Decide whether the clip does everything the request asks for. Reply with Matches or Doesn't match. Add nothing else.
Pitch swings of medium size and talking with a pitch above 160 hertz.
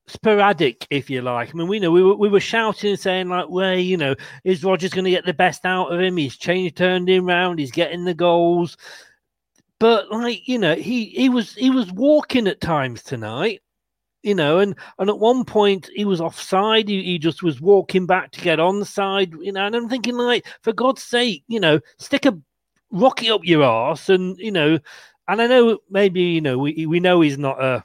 Matches